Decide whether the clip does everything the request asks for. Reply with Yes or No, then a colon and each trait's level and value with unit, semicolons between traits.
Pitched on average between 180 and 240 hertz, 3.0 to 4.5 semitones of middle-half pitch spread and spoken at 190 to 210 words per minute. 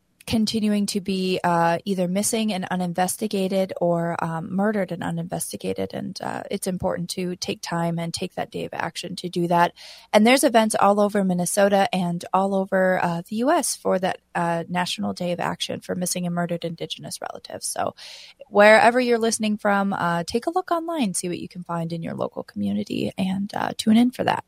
Yes: medium, 185 Hz; average, 3.4 semitones; average, 195 wpm